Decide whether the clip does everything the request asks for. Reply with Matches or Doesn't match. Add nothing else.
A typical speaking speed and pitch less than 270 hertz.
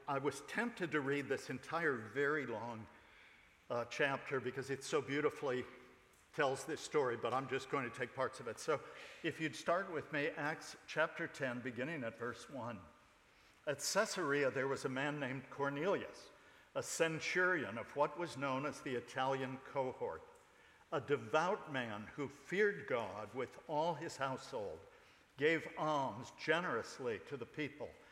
Matches